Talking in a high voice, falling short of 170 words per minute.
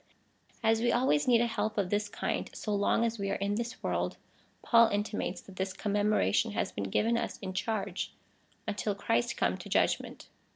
No: high, 205 Hz; average, 190 wpm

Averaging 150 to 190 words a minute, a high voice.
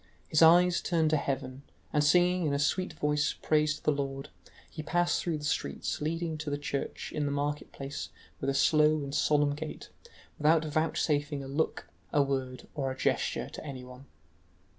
No: average, 185 wpm; medium, 150 Hz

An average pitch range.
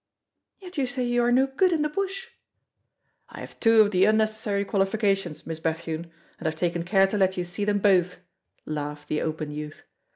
No: wide, 6.3 semitones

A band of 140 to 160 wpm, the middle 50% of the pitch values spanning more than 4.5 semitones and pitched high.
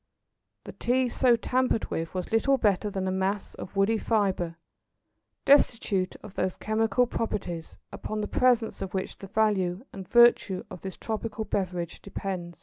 No: average, 155 wpm; average, 3.3 semitones; high, 200 Hz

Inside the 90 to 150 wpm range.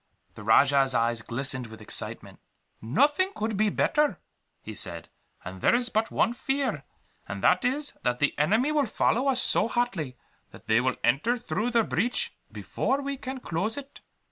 No: average, 170 wpm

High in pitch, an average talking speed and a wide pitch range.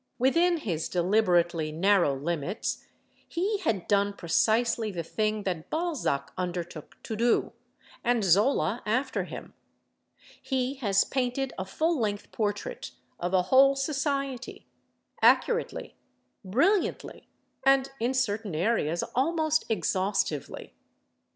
No: high, 220 Hz; slow, 110 wpm; wide, 6.8 semitones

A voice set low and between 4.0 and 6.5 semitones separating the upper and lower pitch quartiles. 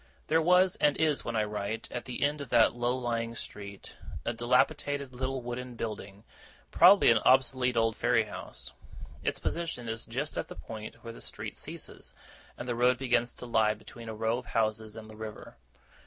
No: low, 120 Hz; average, 2.7 semitones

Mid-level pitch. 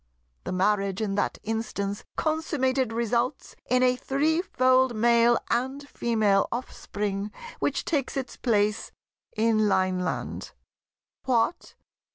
No: high, 235 Hz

